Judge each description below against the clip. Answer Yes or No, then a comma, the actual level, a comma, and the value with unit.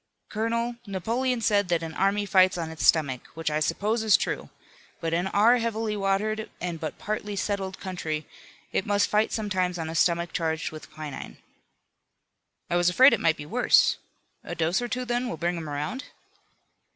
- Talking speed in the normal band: Yes, average, 180 wpm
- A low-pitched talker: No, high, 190 Hz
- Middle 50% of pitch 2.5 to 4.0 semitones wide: No, average, 4.8 semitones